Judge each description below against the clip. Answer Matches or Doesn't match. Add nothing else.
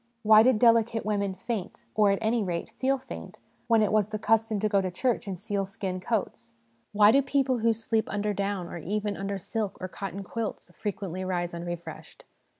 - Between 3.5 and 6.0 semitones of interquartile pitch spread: Doesn't match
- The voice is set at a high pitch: Matches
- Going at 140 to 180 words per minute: Doesn't match